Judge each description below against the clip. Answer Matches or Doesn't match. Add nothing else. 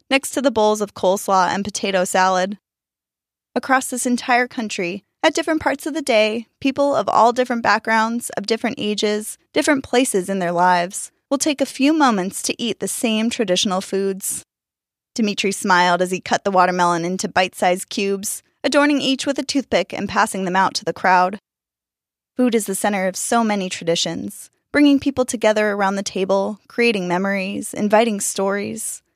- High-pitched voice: Matches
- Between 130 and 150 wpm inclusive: Doesn't match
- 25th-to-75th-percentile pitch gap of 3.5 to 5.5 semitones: Matches